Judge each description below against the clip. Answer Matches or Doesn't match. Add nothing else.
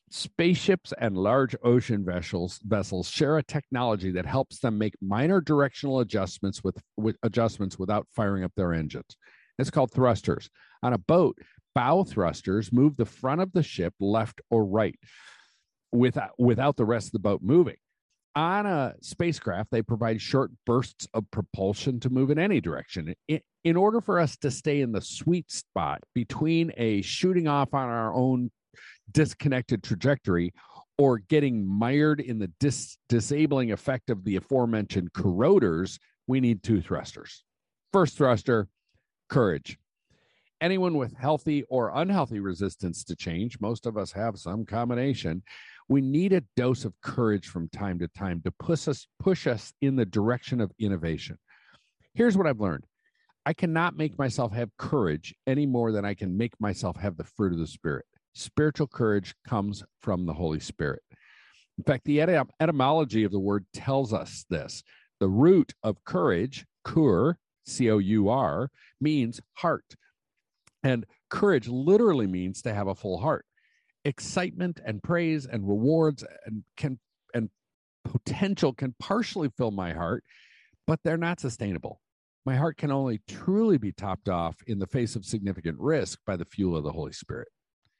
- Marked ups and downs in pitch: Matches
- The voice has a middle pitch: Doesn't match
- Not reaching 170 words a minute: Matches